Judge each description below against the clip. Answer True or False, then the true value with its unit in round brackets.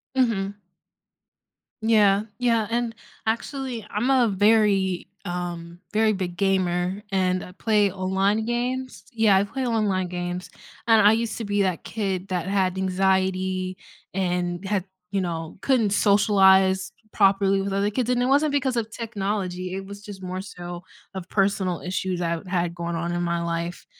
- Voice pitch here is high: True (195 Hz)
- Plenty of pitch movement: False (3.0 semitones)